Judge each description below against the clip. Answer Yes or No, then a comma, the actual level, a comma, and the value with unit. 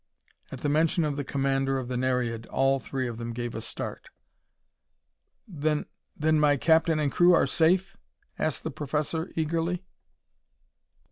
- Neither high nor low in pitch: Yes, medium, 145 Hz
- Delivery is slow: No, average, 150 wpm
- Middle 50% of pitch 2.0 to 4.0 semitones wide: Yes, average, 3.5 semitones